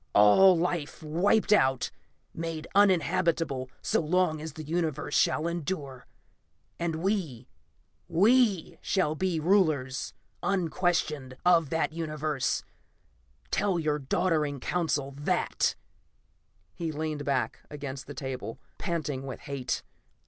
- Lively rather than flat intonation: No, average, 3.8 semitones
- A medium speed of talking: No, slow, 110 wpm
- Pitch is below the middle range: No, medium, 155 Hz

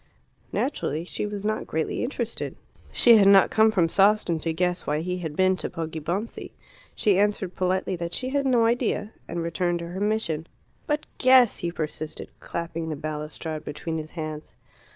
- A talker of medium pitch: Yes, medium, 180 Hz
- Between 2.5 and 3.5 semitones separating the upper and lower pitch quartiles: No, average, 4.7 semitones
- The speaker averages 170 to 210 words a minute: Yes, average, 175 wpm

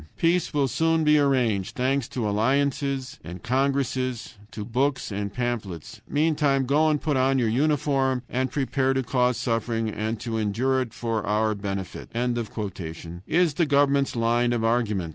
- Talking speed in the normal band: Yes, average, 155 wpm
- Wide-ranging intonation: No, average, 3.7 semitones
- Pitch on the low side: Yes, low, 130 Hz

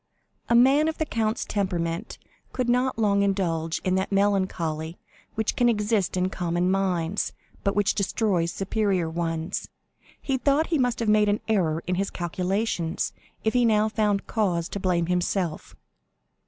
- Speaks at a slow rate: No, average, 155 wpm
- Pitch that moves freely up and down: No, average, 4.0 semitones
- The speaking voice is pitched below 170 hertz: No, high, 195 Hz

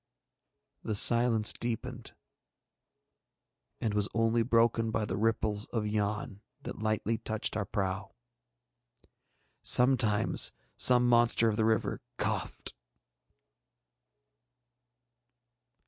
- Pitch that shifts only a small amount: Yes, narrow, 1.8 semitones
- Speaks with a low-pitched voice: Yes, low, 110 Hz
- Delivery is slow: Yes, slow, 90 wpm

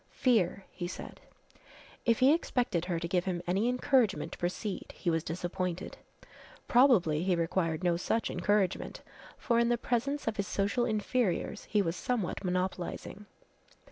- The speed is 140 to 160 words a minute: Yes, average, 150 wpm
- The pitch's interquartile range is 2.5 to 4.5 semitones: No, average, 5.0 semitones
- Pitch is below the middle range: No, high, 195 Hz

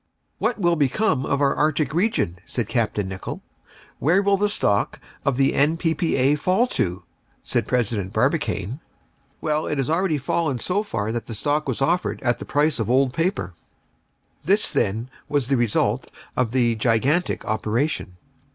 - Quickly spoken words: No, average, 160 wpm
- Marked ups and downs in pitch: Yes, wide, 6.1 semitones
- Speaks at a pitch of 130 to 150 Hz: Yes, medium, 140 Hz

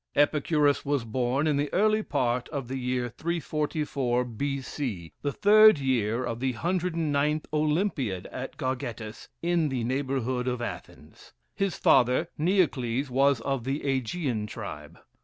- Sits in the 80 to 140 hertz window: Yes, low, 135 Hz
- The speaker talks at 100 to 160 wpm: Yes, average, 140 wpm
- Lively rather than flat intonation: No, average, 3.6 semitones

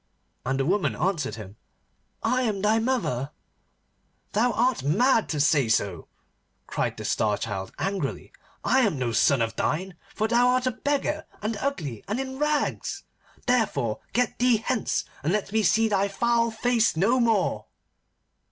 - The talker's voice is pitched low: No, high, 215 Hz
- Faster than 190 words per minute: No, average, 160 wpm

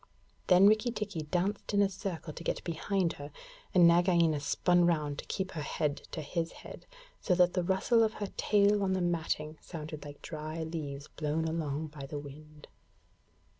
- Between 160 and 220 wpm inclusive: Yes, average, 180 wpm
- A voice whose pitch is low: No, medium, 170 Hz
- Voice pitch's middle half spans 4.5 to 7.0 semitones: No, average, 3.7 semitones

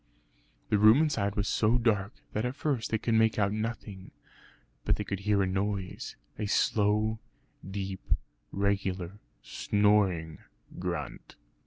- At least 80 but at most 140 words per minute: Yes, slow, 135 wpm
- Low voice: Yes, low, 105 Hz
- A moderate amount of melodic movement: No, narrow, 2.0 semitones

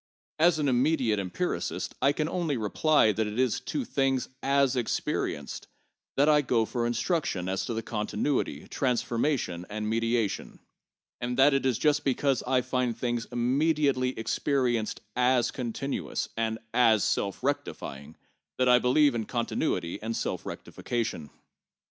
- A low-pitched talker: Yes, low, 125 Hz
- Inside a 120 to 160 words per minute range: Yes, average, 140 wpm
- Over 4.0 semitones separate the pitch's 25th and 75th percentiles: No, average, 3.7 semitones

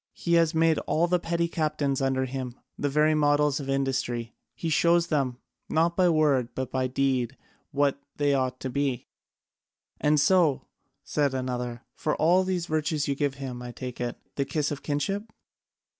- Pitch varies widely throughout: No, average, 3.3 semitones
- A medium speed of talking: Yes, average, 170 wpm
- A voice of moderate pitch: Yes, medium, 145 Hz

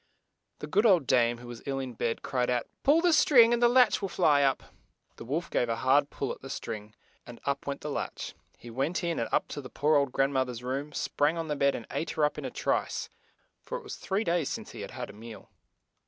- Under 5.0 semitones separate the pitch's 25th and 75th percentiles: No, wide, 5.5 semitones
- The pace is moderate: No, fast, 260 wpm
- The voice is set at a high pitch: No, medium, 140 Hz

